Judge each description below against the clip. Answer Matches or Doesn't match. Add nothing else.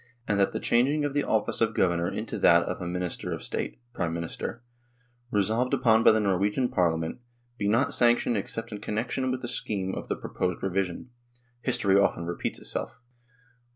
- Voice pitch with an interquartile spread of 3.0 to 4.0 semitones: Doesn't match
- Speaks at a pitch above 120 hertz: Doesn't match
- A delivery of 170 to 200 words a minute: Matches